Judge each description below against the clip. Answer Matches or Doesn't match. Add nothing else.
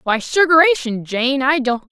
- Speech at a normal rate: Matches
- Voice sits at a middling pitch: Doesn't match